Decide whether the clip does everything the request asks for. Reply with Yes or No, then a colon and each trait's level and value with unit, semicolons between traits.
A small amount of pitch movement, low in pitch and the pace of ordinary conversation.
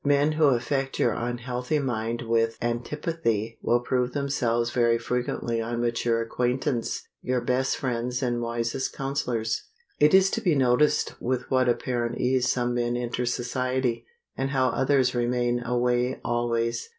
Yes: narrow, 1.8 semitones; low, 125 Hz; average, 145 wpm